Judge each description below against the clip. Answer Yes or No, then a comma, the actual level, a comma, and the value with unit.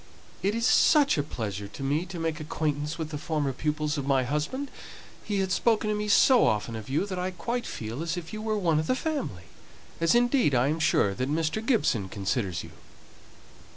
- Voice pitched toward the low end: No, medium, 155 Hz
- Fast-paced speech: Yes, fast, 210 wpm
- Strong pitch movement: Yes, wide, 7.5 semitones